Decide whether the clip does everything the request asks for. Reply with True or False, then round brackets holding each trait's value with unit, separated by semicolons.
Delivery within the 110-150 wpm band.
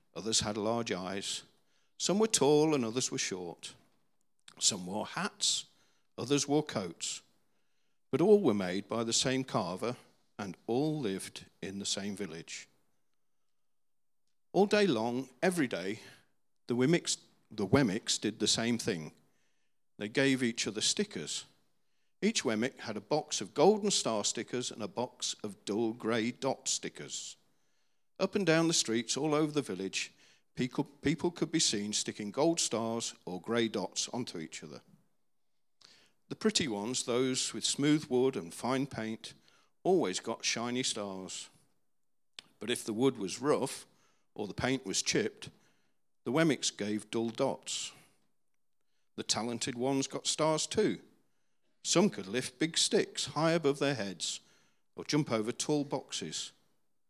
True (145 wpm)